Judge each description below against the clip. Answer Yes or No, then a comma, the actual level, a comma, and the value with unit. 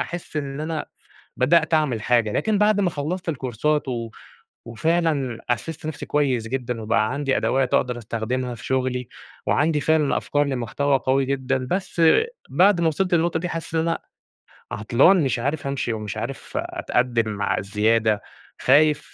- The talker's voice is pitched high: No, low, 135 Hz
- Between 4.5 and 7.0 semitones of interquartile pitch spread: Yes, average, 5.0 semitones